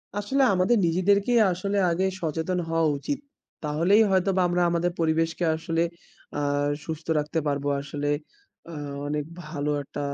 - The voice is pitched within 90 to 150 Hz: No, medium, 165 Hz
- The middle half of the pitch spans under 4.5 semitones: Yes, average, 3.3 semitones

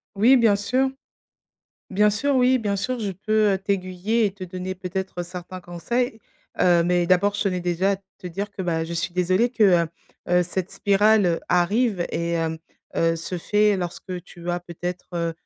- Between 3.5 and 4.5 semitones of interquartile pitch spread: No, average, 2.9 semitones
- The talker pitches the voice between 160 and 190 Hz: Yes, medium, 185 Hz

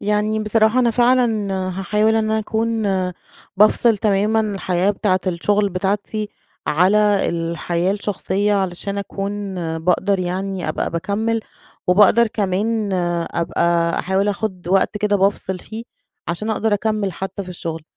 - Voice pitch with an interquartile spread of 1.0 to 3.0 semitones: Yes, average, 2.7 semitones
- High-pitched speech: Yes, high, 200 Hz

